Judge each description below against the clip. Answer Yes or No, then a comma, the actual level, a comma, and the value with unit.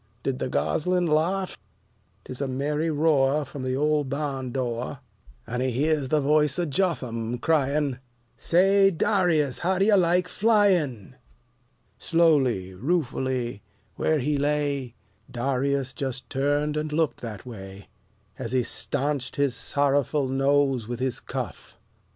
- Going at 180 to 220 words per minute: No, slow, 135 wpm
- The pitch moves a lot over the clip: No, average, 3.2 semitones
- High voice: No, medium, 140 Hz